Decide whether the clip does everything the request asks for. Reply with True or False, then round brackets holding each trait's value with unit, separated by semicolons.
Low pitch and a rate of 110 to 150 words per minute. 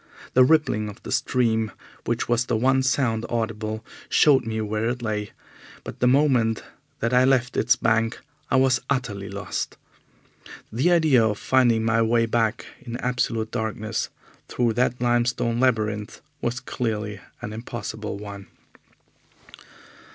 True (115 Hz; 140 wpm)